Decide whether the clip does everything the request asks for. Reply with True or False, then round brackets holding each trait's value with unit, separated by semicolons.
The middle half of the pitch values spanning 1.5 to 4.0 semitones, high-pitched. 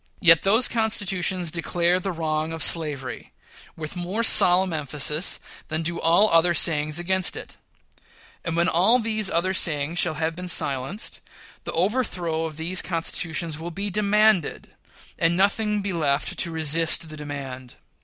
False (3.1 semitones; 170 Hz)